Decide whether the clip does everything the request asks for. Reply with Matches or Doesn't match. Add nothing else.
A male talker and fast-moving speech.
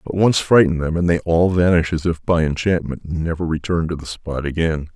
Matches